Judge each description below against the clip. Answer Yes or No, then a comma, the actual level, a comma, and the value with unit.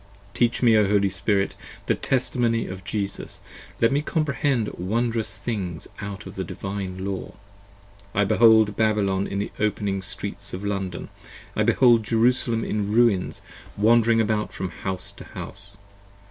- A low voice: Yes, low, 105 Hz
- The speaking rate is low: No, average, 145 wpm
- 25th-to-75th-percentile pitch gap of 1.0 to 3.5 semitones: Yes, average, 2.8 semitones